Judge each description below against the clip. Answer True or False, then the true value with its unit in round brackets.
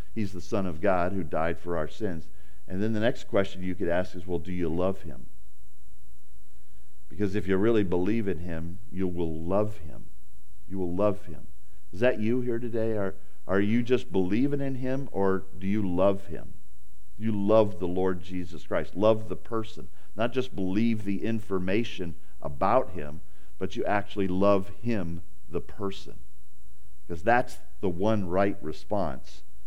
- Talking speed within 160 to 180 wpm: True (170 wpm)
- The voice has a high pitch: False (95 Hz)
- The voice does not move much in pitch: False (3.7 semitones)